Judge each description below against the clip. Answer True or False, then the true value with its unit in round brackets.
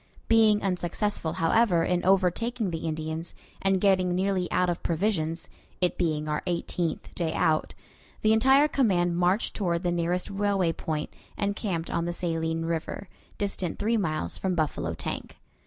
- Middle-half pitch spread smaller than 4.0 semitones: True (3.3 semitones)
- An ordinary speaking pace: True (155 wpm)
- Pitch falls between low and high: True (180 Hz)